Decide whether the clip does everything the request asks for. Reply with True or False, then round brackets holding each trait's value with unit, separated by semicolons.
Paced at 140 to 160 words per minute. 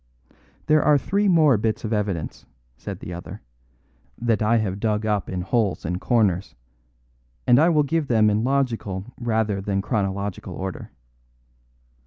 True (150 wpm)